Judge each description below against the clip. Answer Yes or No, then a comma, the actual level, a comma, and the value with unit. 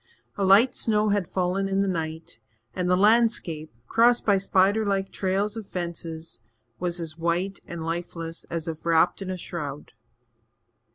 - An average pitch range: Yes, average, 3.0 semitones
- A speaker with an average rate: Yes, average, 160 wpm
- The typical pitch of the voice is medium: Yes, medium, 180 Hz